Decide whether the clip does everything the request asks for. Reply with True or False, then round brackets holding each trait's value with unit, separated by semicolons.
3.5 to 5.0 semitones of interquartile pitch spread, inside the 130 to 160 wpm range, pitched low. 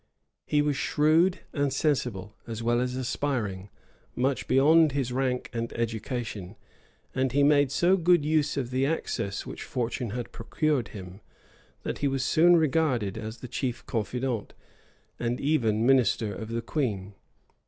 True (4.1 semitones; 150 wpm; 125 Hz)